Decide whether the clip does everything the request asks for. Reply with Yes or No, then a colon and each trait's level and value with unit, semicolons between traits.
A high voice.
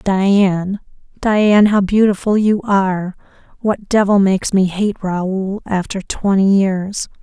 Yes: high, 195 Hz